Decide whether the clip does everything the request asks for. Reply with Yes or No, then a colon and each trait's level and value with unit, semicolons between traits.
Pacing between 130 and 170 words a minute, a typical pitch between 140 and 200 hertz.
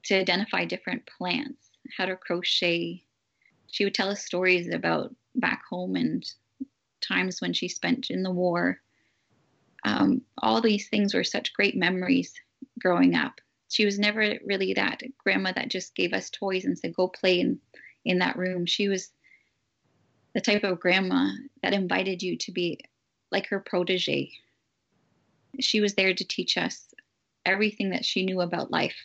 Yes: average, 160 wpm; high, 190 Hz